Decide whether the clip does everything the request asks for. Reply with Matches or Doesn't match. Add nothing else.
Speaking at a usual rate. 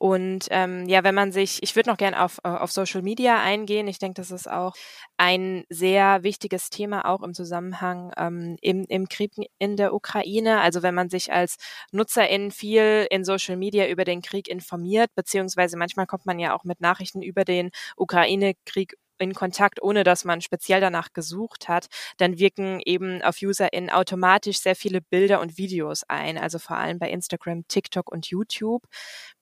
Matches